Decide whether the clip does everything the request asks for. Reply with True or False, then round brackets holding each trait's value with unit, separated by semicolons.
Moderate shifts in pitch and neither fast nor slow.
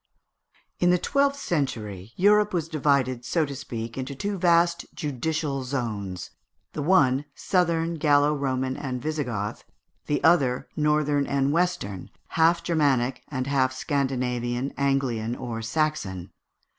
False (4.4 semitones; 125 wpm)